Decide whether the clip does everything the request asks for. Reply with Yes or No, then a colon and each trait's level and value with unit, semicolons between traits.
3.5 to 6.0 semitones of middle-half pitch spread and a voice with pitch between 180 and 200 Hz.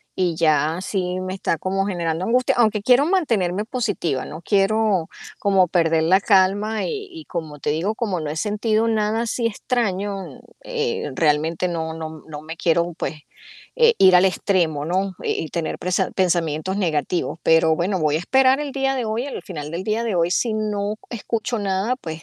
Yes: average, 5.0 semitones; high, 190 Hz